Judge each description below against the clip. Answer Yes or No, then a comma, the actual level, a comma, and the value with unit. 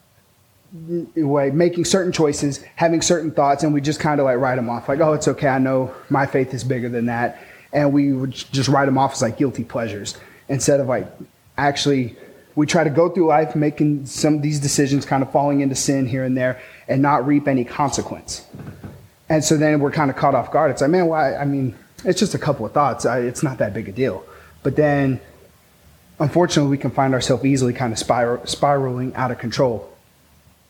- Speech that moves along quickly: Yes, fast, 210 wpm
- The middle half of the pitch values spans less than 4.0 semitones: Yes, average, 2.9 semitones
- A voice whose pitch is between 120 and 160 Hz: Yes, medium, 140 Hz